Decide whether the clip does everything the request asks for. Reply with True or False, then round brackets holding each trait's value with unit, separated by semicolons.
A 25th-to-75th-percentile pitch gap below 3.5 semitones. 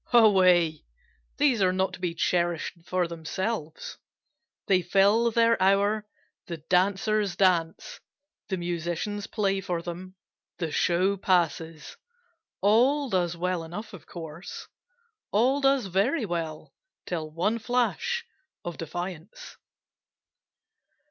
False (3.8 semitones)